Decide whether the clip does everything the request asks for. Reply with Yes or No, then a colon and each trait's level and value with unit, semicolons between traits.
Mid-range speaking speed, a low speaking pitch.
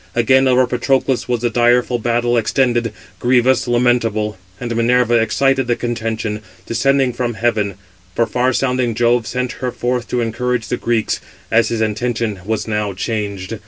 Yes: average, 155 wpm; low, 120 Hz